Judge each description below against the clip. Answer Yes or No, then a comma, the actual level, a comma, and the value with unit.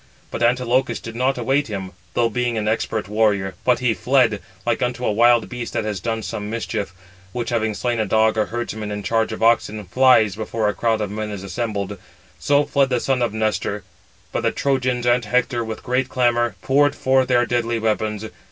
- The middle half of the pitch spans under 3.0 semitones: Yes, narrow, 2.5 semitones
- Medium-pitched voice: No, low, 115 Hz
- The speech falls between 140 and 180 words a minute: No, average, 200 wpm